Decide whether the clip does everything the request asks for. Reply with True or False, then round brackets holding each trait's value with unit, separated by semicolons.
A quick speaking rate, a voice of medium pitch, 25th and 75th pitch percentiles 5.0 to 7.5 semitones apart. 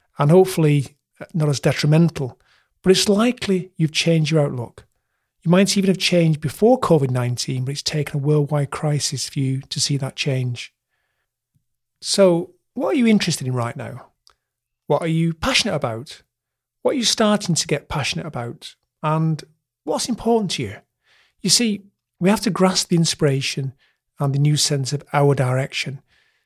False (165 wpm; 150 Hz; 5.3 semitones)